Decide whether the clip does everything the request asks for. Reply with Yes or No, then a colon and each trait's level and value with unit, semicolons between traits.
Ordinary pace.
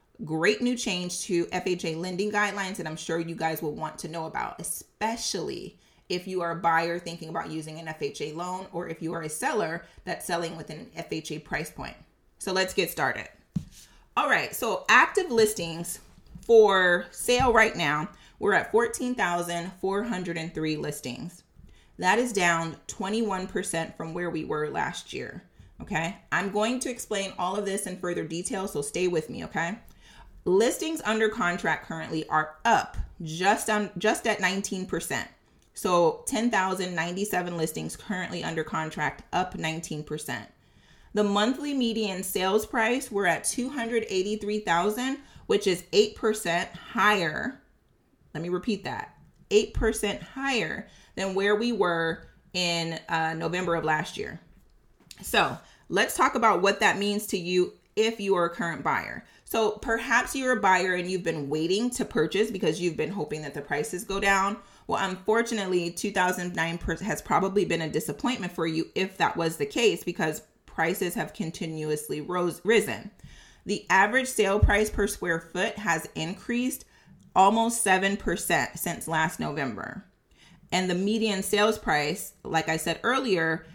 Yes: average, 150 wpm